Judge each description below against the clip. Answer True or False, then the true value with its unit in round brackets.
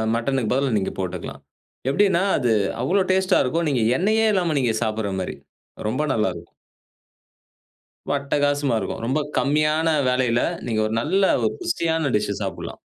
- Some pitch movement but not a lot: False (6.3 semitones)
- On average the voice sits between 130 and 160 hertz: True (140 Hz)